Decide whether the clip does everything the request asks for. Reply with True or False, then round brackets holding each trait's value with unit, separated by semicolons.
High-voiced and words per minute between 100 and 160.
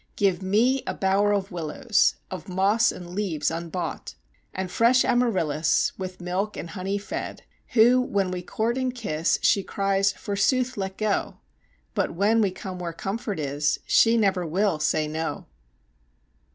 True (195 Hz; 150 wpm)